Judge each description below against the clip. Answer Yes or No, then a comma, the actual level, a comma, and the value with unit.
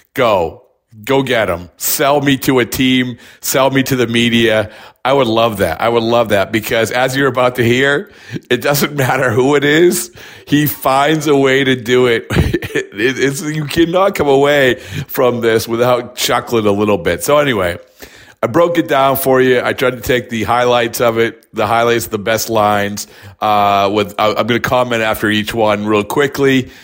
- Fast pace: No, average, 190 wpm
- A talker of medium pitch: No, low, 125 Hz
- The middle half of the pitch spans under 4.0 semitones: Yes, average, 3.3 semitones